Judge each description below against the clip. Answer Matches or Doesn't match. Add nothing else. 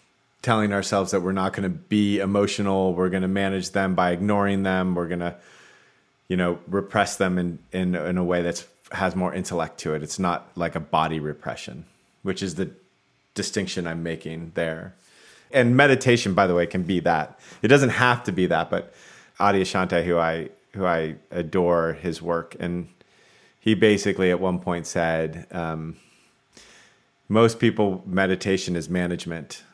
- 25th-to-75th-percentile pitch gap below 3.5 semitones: Matches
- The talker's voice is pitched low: Matches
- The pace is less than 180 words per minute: Matches